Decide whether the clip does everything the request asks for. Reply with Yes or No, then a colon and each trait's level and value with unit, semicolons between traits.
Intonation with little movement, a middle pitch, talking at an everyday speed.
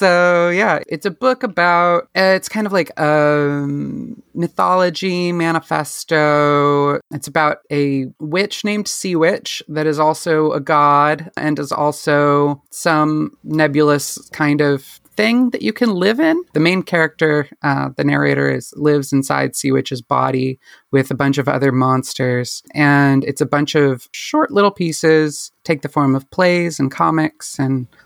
No: average, 3.5 semitones; medium, 150 Hz; average, 155 wpm